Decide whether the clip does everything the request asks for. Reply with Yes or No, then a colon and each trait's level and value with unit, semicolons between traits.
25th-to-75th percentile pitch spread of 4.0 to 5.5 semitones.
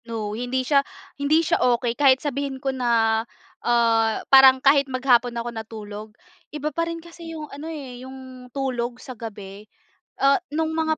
No: average, 3.3 semitones